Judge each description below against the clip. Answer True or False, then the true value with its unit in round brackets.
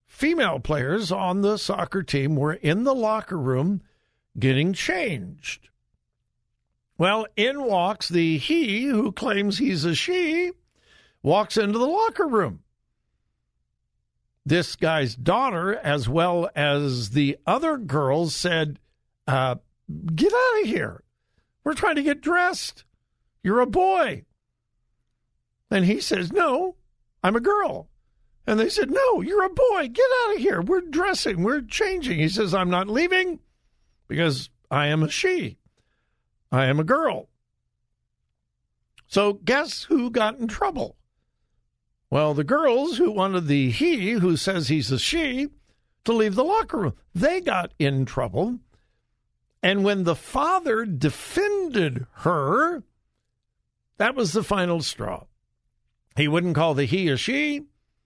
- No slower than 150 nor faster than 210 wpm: False (135 wpm)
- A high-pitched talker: True (200 Hz)